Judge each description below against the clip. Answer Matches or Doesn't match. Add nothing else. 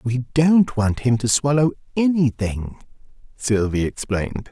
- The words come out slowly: Matches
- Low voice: Matches